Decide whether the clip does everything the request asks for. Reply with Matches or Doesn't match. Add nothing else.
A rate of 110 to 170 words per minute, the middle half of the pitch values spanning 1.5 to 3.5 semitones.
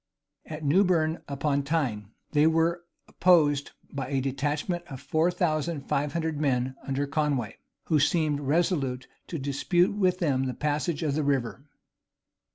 Matches